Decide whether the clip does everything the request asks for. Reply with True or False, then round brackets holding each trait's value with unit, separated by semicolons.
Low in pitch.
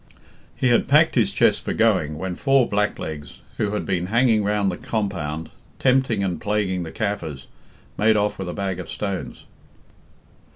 True (100 Hz)